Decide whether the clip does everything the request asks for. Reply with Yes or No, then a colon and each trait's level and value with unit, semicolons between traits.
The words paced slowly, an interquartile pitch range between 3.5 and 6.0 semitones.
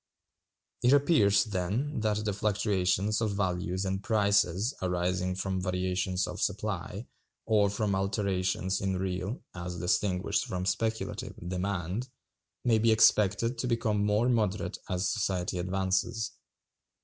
No: slow, 125 wpm; average, 2.7 semitones